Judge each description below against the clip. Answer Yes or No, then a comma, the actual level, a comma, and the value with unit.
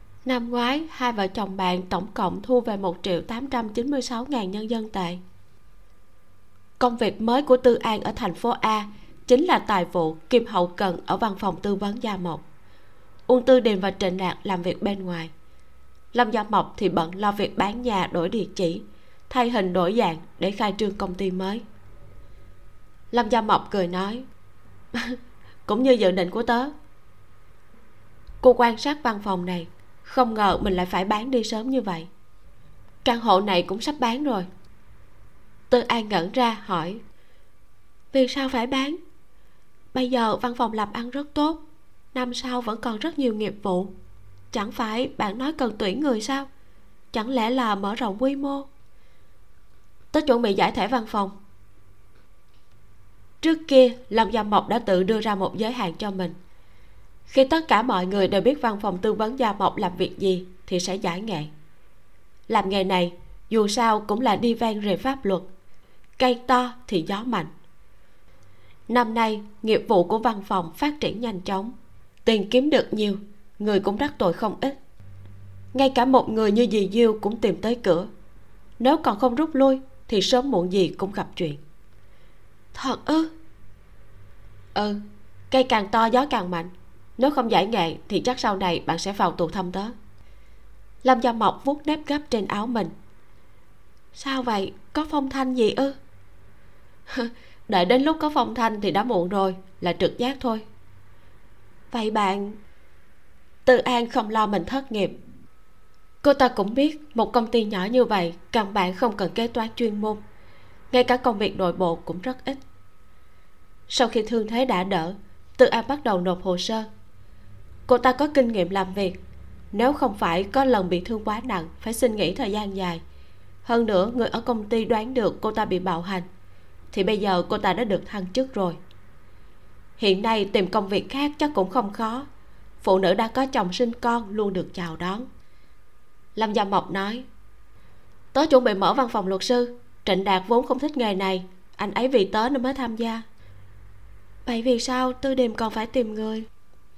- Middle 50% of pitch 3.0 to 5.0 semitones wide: No, wide, 5.5 semitones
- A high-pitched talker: Yes, high, 210 Hz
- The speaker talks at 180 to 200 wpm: Yes, average, 185 wpm